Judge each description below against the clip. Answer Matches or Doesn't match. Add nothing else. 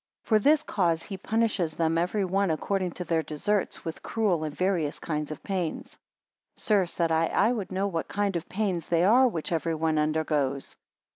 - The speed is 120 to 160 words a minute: Doesn't match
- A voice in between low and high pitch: Matches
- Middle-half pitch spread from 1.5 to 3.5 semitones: Doesn't match